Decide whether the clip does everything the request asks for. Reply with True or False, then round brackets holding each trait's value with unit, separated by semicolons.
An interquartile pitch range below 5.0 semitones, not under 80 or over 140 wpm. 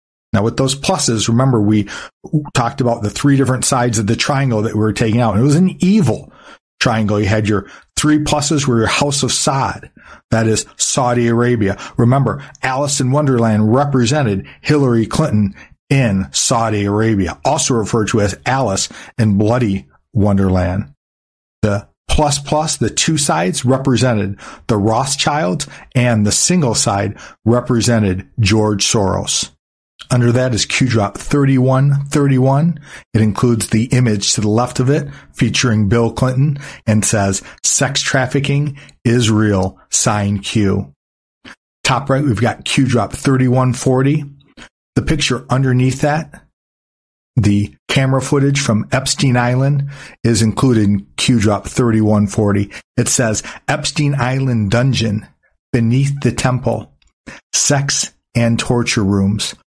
True (4.5 semitones; 135 wpm)